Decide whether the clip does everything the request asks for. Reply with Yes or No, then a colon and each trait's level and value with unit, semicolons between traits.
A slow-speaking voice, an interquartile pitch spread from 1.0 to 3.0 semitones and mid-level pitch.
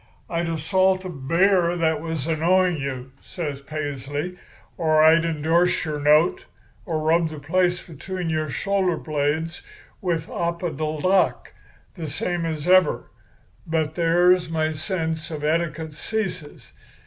Yes: slow, 125 wpm; narrow, 2.4 semitones; medium, 160 Hz